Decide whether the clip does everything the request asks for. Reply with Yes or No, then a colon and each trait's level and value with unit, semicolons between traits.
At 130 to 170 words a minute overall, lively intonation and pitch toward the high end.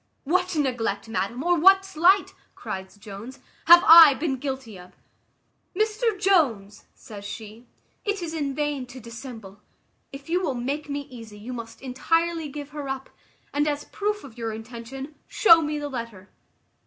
Yes: average, 165 wpm; wide, 6.0 semitones; very high, 275 Hz